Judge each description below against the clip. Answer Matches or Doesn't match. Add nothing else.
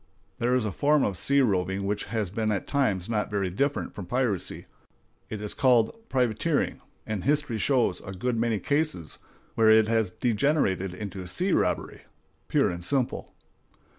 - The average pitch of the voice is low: Matches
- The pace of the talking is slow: Doesn't match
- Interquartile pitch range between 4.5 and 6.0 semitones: Matches